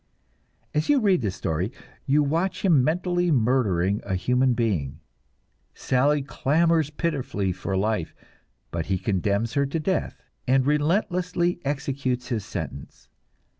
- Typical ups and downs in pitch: No, wide, 7.9 semitones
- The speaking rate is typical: No, slow, 130 wpm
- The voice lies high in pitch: No, low, 135 Hz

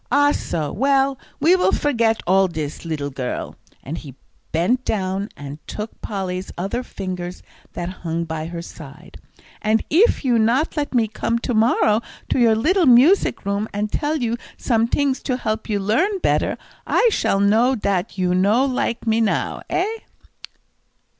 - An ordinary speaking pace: Yes, average, 160 wpm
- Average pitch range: No, wide, 6.0 semitones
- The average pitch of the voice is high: Yes, high, 220 Hz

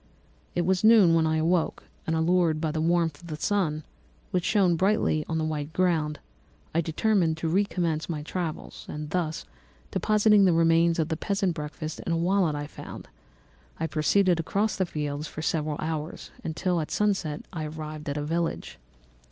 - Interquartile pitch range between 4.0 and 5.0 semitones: No, average, 2.8 semitones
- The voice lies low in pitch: No, medium, 165 Hz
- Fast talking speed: No, average, 175 wpm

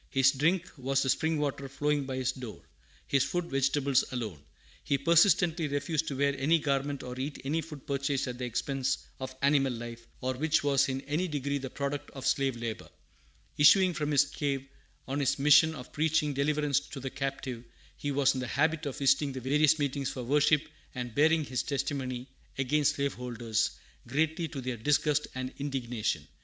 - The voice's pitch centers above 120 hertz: Yes, medium, 140 Hz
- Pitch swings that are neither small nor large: No, narrow, 2.3 semitones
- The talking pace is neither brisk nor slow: Yes, average, 180 wpm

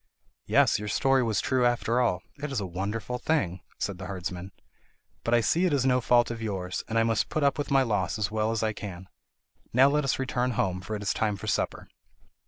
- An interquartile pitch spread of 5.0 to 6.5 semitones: No, average, 4.5 semitones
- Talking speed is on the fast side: Yes, fast, 230 wpm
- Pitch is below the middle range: Yes, low, 115 Hz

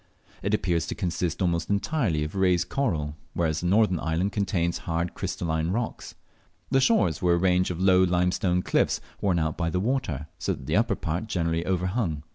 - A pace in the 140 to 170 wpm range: No, average, 185 wpm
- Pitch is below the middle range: Yes, very low, 90 Hz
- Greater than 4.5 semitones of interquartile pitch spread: No, average, 2.7 semitones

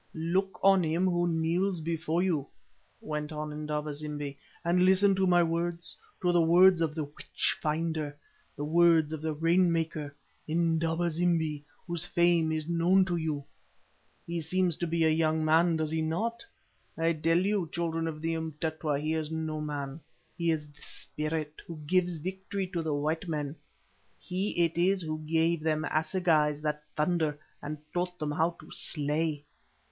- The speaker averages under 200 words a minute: Yes, average, 170 wpm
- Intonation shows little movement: Yes, narrow, 2.1 semitones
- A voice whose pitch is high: No, medium, 160 Hz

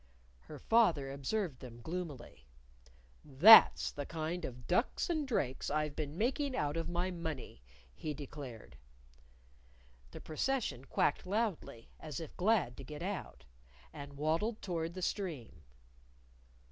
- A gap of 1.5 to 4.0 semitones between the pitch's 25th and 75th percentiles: No, average, 5.1 semitones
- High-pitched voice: No, medium, 155 Hz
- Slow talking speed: Yes, slow, 130 wpm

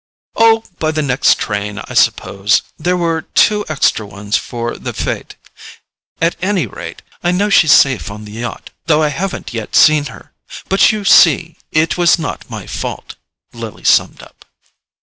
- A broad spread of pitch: Yes, wide, 7.8 semitones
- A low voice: No, medium, 155 Hz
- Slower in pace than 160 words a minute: No, average, 170 wpm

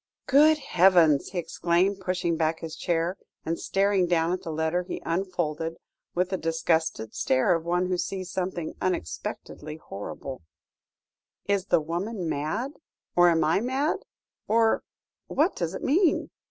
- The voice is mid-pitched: Yes, medium, 175 Hz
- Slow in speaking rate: No, average, 145 wpm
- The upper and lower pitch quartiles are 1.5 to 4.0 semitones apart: Yes, average, 3.0 semitones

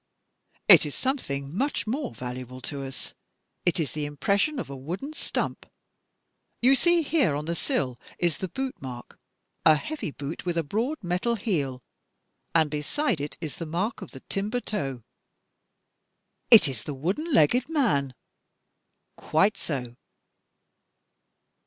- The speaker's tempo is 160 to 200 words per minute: No, average, 145 wpm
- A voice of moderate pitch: Yes, medium, 170 Hz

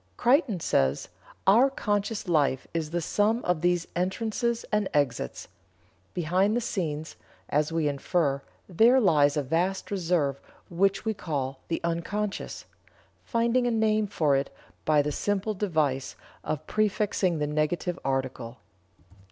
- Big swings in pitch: Yes, wide, 5.9 semitones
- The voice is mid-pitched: Yes, medium, 175 Hz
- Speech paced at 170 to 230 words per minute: No, slow, 135 wpm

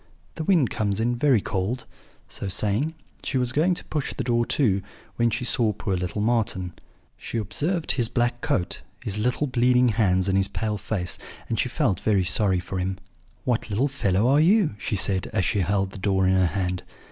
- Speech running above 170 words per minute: Yes, average, 200 wpm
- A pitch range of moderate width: Yes, average, 4.7 semitones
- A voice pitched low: Yes, low, 110 Hz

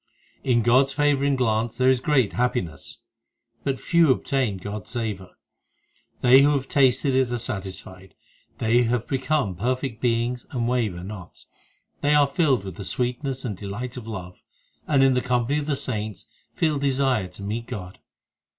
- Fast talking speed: No, average, 170 wpm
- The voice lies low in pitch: Yes, low, 125 Hz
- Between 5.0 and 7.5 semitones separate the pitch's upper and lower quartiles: No, average, 4.1 semitones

